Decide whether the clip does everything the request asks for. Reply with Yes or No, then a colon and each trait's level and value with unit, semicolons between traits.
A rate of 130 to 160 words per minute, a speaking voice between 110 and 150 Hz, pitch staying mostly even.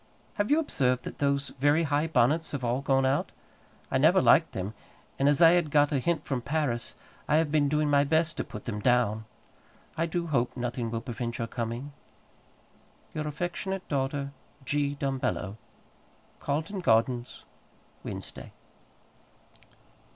No: average, 150 wpm; medium, 140 Hz; average, 3.9 semitones